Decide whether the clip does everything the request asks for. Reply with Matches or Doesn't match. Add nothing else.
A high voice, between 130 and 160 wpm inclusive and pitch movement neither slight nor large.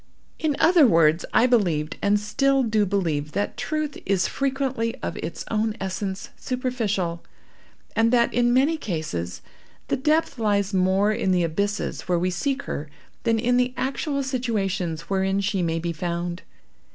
Doesn't match